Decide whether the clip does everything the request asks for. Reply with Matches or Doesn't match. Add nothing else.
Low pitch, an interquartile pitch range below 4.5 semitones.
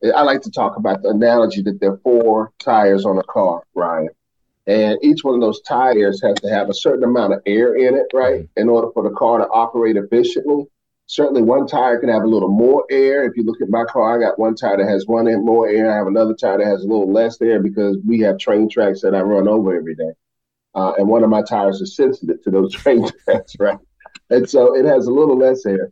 Matches